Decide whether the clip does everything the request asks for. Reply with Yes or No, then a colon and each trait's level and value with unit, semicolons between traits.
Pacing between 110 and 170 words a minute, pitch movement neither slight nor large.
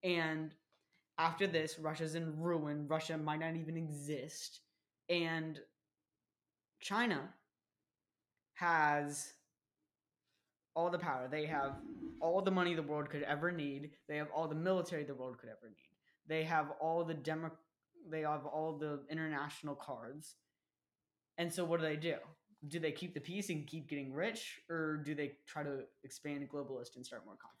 No: average, 160 wpm; narrow, 1.9 semitones